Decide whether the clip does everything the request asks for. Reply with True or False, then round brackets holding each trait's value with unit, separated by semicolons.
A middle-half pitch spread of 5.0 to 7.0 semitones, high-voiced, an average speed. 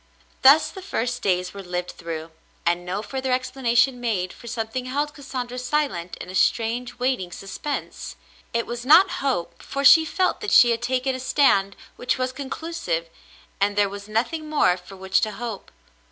True (5.4 semitones; 240 Hz; 175 wpm)